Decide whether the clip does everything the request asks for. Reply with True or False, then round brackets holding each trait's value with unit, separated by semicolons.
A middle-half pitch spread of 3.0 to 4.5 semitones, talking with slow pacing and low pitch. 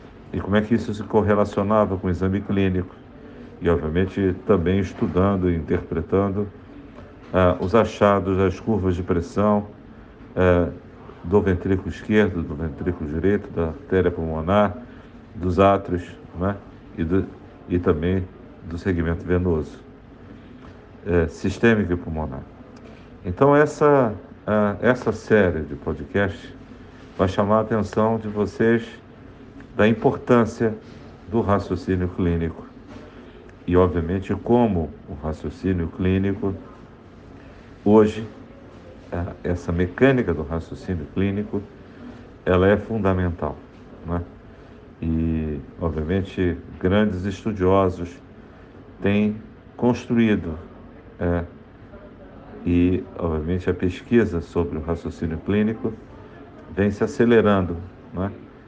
True (3.5 semitones; 105 wpm; 95 Hz)